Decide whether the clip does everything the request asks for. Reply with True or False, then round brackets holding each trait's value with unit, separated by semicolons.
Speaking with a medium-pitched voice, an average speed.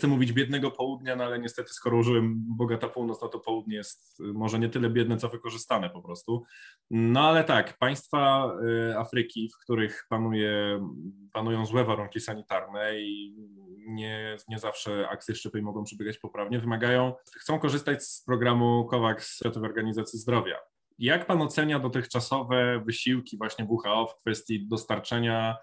False (115 Hz; 145 wpm)